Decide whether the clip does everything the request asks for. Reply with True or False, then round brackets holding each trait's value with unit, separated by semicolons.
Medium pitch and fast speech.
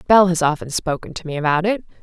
True (170 Hz; 235 wpm)